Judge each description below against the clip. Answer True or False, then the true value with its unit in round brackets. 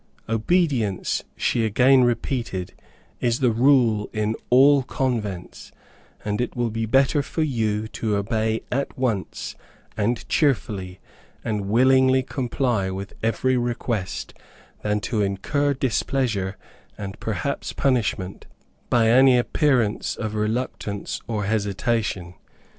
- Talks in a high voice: False (115 Hz)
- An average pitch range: True (3.7 semitones)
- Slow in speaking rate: True (115 wpm)